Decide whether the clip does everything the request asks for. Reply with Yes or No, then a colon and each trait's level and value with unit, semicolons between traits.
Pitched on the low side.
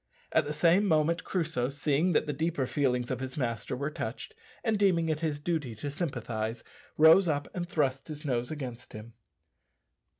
No: medium, 150 Hz